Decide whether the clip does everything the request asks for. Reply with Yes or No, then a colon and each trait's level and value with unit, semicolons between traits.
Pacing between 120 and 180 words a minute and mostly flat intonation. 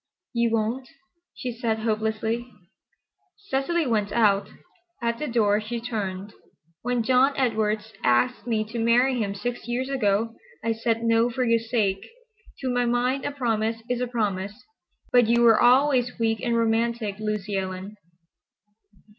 Yes: average, 145 wpm; narrow, 2.3 semitones